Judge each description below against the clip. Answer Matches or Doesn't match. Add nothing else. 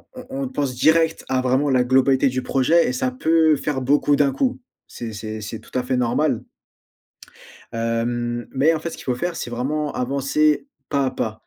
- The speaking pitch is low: Matches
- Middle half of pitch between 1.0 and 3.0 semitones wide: Doesn't match